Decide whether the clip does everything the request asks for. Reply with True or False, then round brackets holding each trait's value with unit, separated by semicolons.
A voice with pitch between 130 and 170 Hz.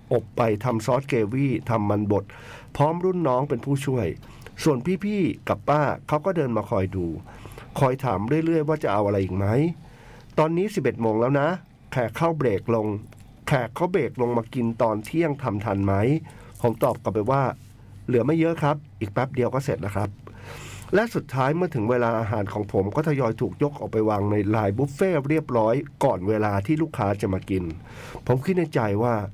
False (120 Hz)